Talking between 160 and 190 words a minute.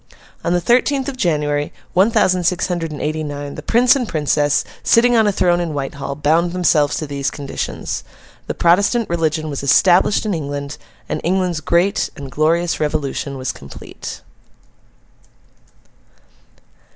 No: average, 150 wpm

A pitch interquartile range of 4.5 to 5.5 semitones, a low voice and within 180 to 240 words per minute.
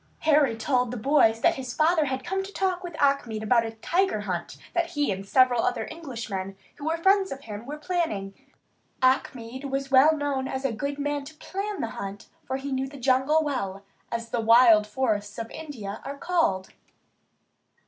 No: average, 5.2 semitones; very high, 265 Hz; average, 190 wpm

